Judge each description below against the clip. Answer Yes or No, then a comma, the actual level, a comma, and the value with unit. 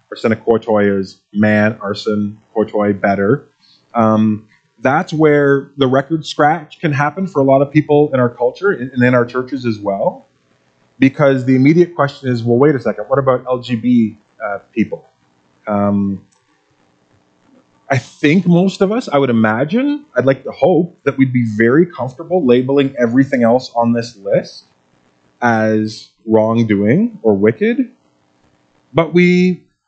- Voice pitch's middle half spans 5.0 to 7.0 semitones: Yes, wide, 5.6 semitones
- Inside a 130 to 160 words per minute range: Yes, average, 150 wpm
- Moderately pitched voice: No, low, 125 Hz